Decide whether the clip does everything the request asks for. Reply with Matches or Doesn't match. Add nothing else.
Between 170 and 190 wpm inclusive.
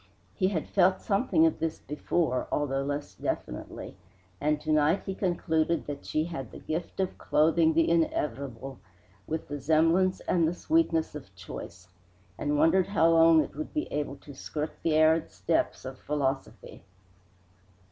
Doesn't match